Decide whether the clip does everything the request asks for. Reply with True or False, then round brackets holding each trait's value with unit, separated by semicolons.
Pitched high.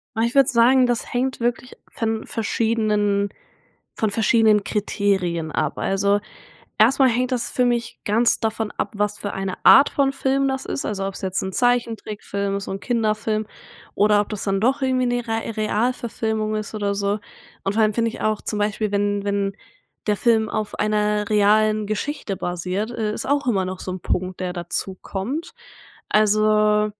True (215 Hz)